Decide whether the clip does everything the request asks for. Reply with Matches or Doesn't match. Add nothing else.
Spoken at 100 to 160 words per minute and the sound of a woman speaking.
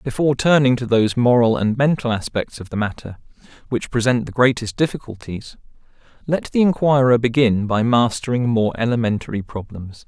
Doesn't match